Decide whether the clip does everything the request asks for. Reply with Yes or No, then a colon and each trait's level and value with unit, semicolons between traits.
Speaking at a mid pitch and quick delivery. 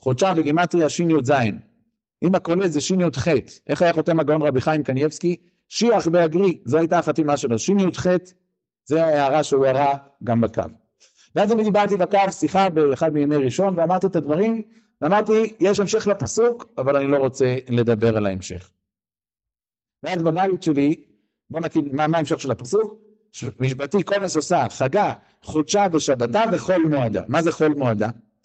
Yes: medium, 160 Hz; fast, 155 wpm